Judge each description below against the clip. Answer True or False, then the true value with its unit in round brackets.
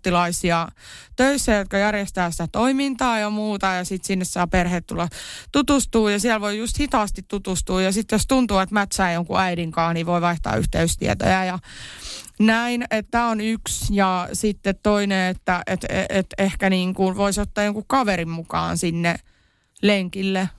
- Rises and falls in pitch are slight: False (3.0 semitones)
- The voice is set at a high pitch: True (195 Hz)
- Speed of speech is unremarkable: False (160 wpm)